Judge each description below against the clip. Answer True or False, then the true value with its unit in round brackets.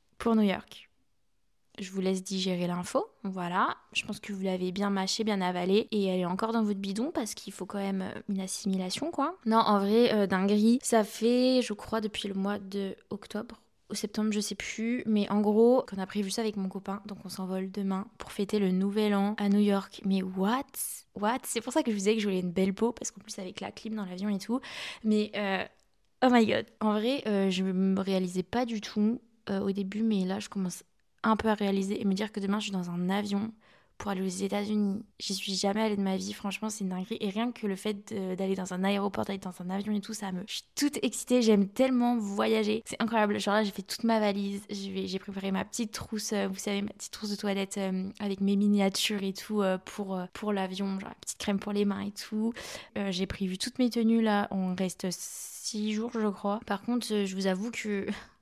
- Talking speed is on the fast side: True (235 wpm)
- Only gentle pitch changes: True (2.0 semitones)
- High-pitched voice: True (205 Hz)